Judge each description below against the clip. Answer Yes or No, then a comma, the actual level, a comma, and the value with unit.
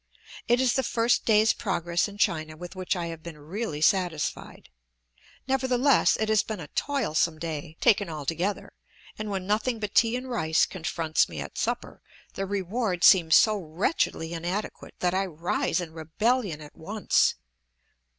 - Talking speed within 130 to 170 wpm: Yes, average, 160 wpm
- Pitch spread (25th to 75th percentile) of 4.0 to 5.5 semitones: Yes, average, 5.1 semitones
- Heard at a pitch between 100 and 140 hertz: No, medium, 185 Hz